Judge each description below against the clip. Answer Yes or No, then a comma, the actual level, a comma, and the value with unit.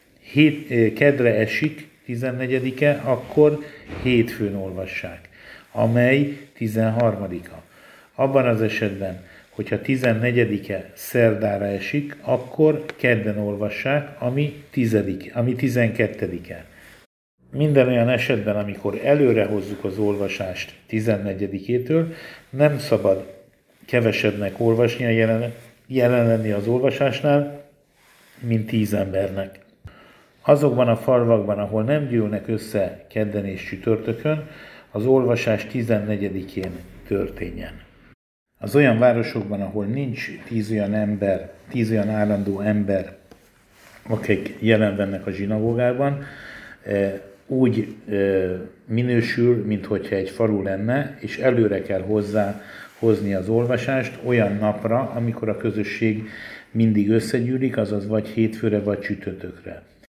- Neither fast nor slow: No, slow, 100 wpm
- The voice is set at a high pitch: No, low, 110 Hz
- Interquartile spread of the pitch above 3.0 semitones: Yes, average, 3.5 semitones